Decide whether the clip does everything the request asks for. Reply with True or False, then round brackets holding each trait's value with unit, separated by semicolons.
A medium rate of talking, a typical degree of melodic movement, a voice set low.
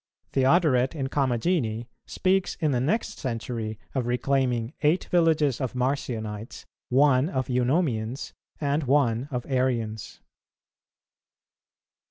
False (105 wpm; 3.4 semitones; 130 Hz)